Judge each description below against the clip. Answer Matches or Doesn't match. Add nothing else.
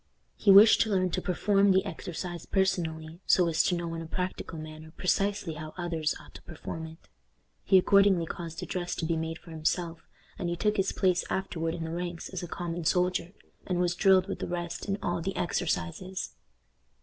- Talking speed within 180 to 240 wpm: Matches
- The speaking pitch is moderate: Matches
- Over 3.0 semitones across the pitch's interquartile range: Doesn't match